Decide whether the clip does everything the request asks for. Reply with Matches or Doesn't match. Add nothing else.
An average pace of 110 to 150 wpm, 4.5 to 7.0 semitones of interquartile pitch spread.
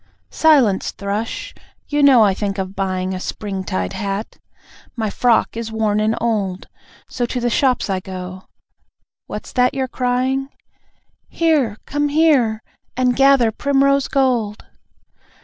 Matches